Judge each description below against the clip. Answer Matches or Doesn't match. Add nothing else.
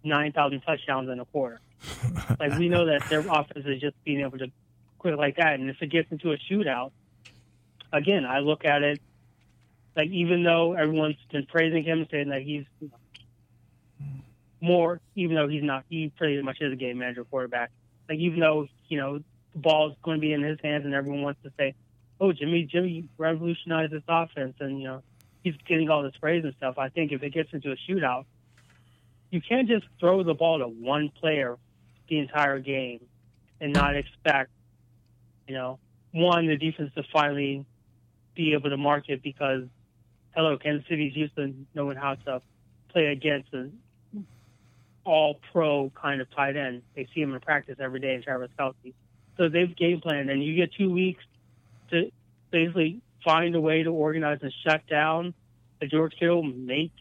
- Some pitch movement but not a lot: Matches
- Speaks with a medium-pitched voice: Matches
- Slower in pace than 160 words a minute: Doesn't match